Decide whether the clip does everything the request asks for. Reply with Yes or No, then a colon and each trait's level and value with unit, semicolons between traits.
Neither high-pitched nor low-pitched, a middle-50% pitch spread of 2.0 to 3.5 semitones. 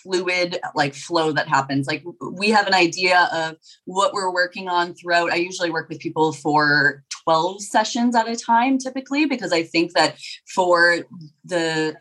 Yes: medium, 175 Hz; average, 2.9 semitones